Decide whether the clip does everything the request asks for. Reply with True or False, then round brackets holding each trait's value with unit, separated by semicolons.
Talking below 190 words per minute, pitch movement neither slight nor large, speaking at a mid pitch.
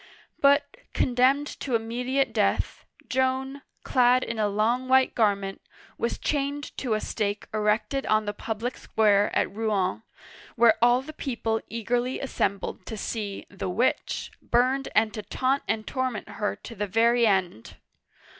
False (150 wpm; 3.5 semitones; 230 Hz)